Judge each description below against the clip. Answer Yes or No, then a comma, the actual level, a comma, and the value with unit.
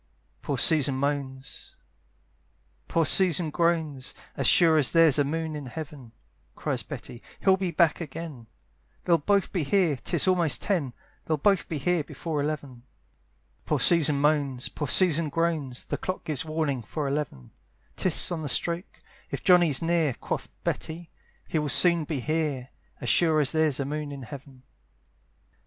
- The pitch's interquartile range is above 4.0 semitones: No, average, 3.2 semitones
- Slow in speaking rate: No, average, 155 wpm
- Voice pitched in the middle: Yes, medium, 155 Hz